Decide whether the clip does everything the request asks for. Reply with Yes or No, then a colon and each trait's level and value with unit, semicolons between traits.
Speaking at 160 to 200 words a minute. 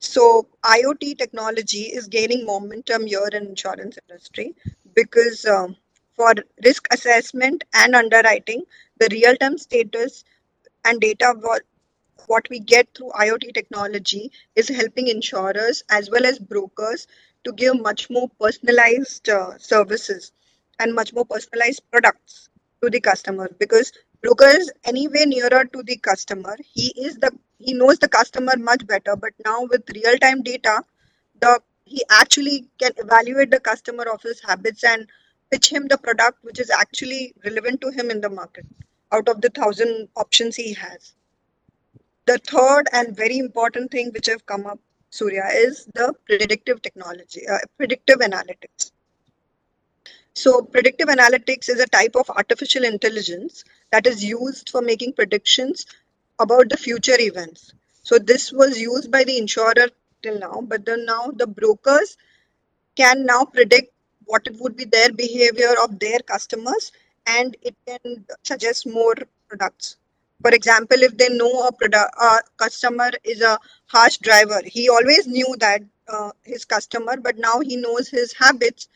No: average, 150 wpm